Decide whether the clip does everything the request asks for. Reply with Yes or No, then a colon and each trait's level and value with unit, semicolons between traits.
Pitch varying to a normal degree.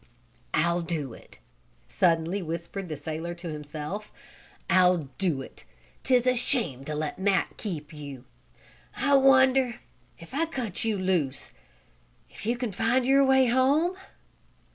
No: wide, 8.1 semitones